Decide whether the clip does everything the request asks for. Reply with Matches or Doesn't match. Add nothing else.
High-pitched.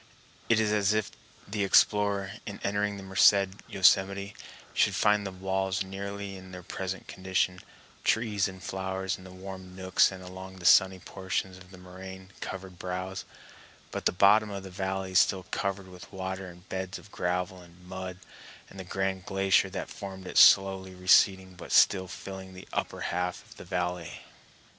Doesn't match